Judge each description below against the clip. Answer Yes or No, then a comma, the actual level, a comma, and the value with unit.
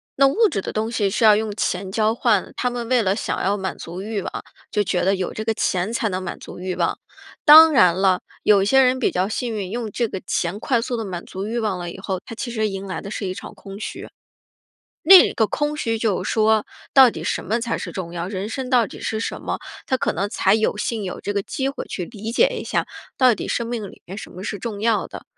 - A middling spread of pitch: Yes, average, 3.6 semitones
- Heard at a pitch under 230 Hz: Yes, high, 215 Hz